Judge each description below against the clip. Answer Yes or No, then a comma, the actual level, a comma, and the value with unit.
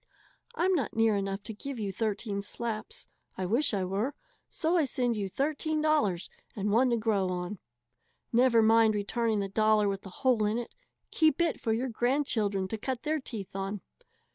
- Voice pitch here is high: Yes, high, 225 Hz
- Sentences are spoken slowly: No, average, 185 wpm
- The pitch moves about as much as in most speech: Yes, average, 4.6 semitones